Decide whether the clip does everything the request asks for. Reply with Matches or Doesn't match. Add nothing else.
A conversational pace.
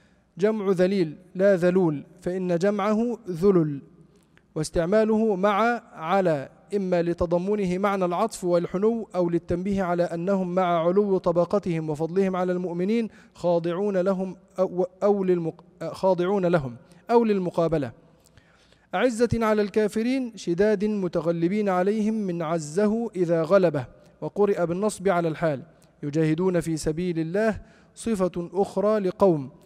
Matches